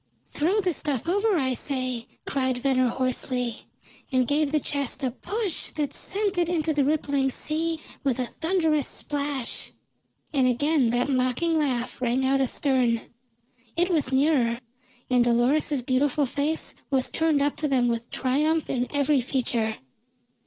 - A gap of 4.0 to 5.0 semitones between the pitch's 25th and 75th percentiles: No, average, 3.5 semitones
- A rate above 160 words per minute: No, average, 150 wpm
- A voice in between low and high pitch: No, very high, 275 Hz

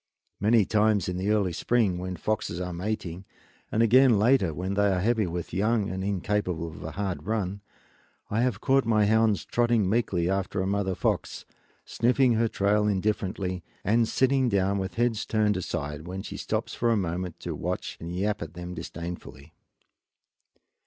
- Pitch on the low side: Yes, low, 100 Hz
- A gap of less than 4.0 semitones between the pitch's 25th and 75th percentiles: Yes, average, 3.4 semitones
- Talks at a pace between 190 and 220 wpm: No, average, 175 wpm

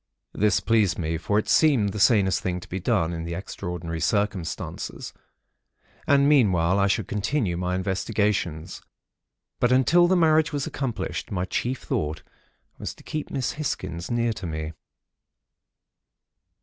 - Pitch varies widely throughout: Yes, wide, 6.1 semitones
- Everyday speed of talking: Yes, average, 145 wpm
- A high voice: No, low, 100 Hz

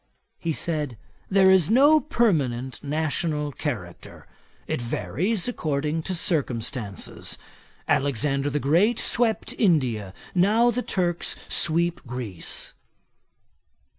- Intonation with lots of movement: Yes, wide, 6.3 semitones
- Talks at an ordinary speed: No, slow, 100 wpm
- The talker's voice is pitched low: No, medium, 155 Hz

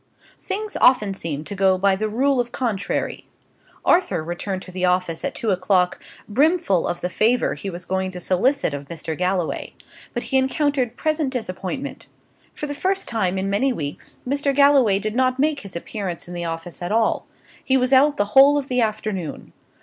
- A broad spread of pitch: Yes, wide, 6.7 semitones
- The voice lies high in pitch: Yes, high, 215 Hz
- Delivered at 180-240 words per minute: Yes, average, 190 wpm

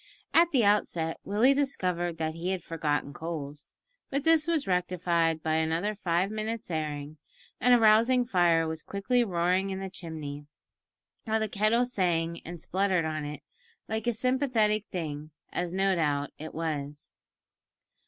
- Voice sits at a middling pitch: Yes, medium, 180 Hz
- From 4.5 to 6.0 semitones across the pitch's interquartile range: Yes, average, 5.2 semitones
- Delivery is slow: No, average, 155 wpm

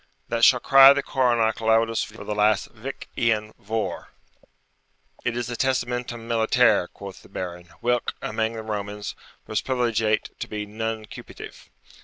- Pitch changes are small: Yes, narrow, 2.1 semitones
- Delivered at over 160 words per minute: No, average, 150 wpm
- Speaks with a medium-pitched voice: No, low, 115 Hz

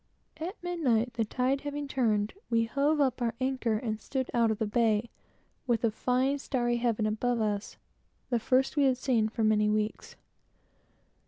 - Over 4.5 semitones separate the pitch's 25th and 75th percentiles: No, average, 3.3 semitones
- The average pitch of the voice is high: Yes, high, 240 Hz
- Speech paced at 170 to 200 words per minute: Yes, average, 175 wpm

